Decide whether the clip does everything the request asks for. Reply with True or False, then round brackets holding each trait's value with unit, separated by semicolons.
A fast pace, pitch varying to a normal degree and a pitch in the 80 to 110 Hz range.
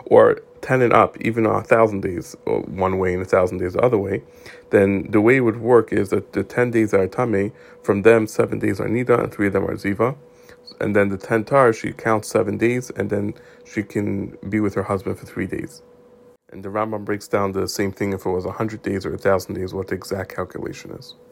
True (240 wpm; 3.1 semitones; 105 Hz)